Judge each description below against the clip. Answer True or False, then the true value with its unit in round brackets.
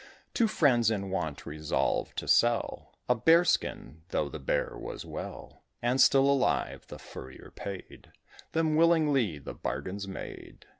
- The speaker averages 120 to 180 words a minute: True (145 wpm)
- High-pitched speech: False (120 Hz)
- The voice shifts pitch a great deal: True (8.2 semitones)